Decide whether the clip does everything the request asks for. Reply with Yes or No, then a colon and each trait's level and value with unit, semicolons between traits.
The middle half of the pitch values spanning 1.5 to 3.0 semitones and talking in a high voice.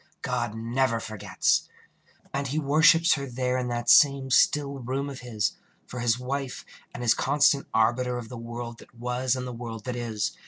No: narrow, 2.6 semitones; low, 125 Hz